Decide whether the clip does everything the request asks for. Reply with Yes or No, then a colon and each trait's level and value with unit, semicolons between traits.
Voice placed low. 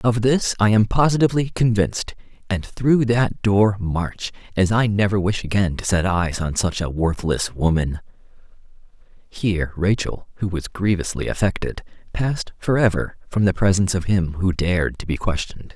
Yes: low, 100 Hz